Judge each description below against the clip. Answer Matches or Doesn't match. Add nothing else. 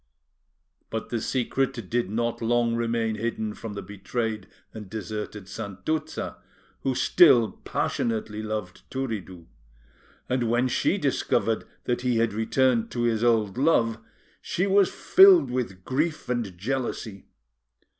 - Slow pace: Matches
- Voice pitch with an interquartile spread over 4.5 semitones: Doesn't match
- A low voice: Matches